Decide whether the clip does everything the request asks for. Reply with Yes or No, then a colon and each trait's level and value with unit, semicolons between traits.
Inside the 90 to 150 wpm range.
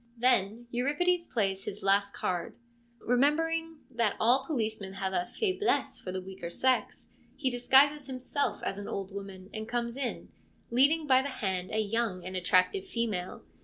No: average, 165 wpm